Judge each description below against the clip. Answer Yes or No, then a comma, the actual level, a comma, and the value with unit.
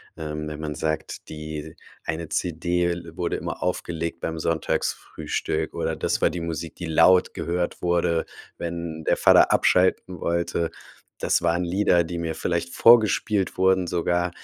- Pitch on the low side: Yes, very low, 85 Hz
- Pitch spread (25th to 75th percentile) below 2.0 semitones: Yes, narrow, 1.6 semitones